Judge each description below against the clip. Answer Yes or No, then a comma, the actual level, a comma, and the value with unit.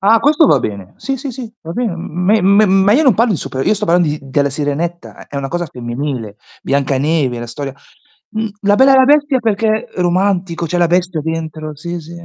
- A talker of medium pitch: Yes, medium, 175 Hz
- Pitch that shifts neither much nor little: No, wide, 6.8 semitones